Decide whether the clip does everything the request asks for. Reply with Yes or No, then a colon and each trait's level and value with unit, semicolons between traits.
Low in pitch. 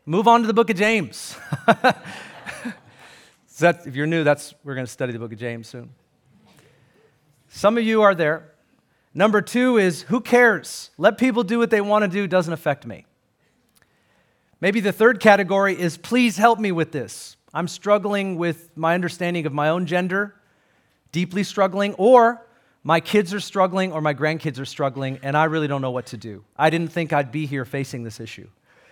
No: medium, 170 Hz